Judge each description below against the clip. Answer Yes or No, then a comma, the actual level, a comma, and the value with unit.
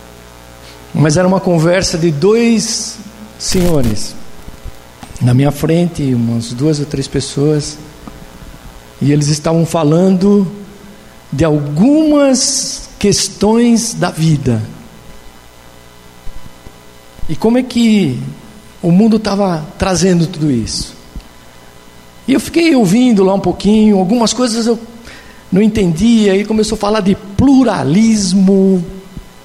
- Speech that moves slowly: Yes, slow, 105 wpm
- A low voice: No, medium, 175 Hz